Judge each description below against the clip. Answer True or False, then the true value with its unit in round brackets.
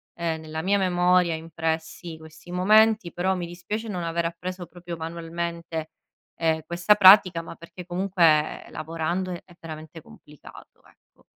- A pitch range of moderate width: False (2.0 semitones)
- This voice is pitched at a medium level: True (170 Hz)